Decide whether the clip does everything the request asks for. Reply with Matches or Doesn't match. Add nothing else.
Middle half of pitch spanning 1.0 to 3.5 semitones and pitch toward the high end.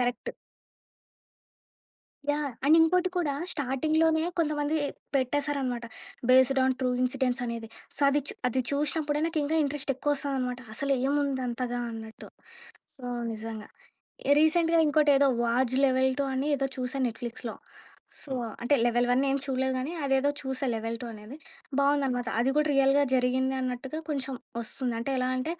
Matches